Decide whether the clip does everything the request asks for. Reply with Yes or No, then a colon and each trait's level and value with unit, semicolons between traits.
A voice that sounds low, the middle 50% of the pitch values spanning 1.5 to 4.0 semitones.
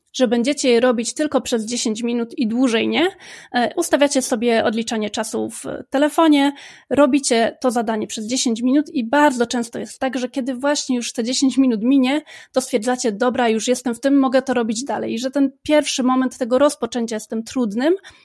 No: very high, 255 Hz; average, 2.8 semitones